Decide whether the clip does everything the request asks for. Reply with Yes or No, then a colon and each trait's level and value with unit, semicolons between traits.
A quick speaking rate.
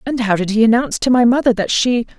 Yes: fast, 275 wpm